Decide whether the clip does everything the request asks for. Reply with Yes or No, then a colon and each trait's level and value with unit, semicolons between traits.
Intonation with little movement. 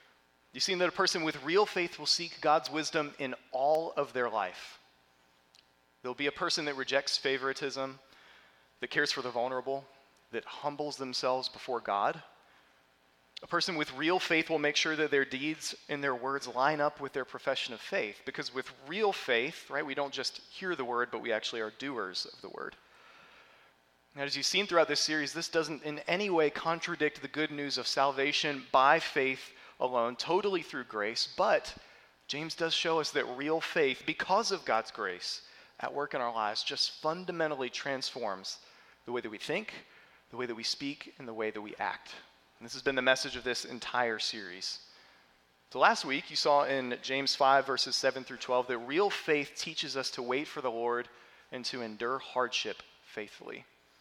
No: average, 3.9 semitones